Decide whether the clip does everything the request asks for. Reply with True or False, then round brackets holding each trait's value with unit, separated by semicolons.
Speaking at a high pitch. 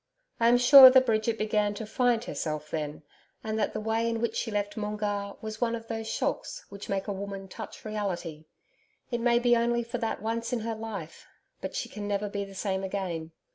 True (215 Hz)